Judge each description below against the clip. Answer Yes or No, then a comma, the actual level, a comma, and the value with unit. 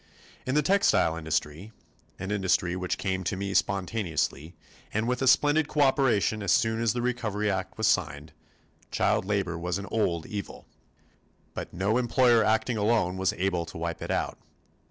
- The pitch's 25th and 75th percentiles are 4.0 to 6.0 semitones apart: Yes, average, 4.5 semitones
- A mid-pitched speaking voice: No, low, 100 Hz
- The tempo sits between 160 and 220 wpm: Yes, average, 165 wpm